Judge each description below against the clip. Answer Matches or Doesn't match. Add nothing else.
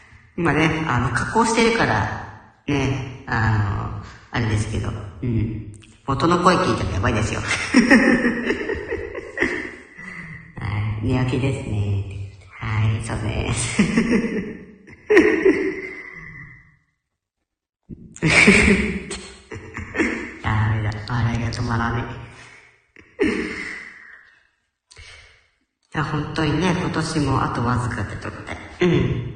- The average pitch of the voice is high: Doesn't match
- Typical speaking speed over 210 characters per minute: Doesn't match